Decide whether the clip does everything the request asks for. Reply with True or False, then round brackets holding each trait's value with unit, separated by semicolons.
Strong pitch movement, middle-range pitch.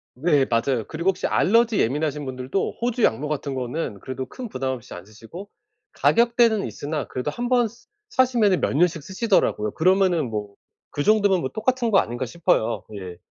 True (8.8 semitones; 155 Hz)